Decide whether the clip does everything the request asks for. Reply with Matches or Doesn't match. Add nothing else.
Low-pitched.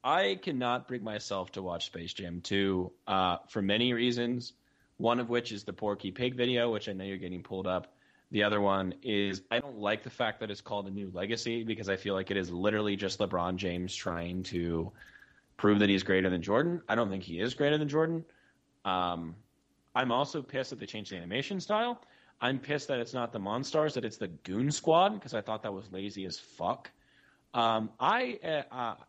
Matches